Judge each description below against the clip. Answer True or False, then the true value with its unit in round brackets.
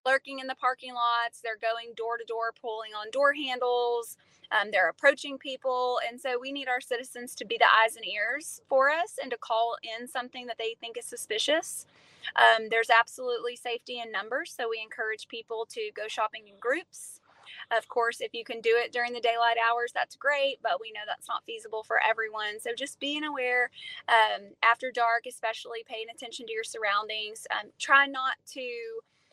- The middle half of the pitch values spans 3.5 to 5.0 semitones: False (2.7 semitones)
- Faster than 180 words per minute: True (195 wpm)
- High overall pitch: True (240 Hz)